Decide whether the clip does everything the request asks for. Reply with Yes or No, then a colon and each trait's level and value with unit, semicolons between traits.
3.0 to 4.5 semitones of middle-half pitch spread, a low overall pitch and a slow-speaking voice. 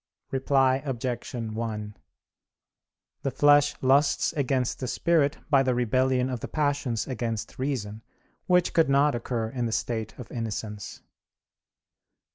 Yes: average, 3.4 semitones; low, 130 Hz; slow, 125 wpm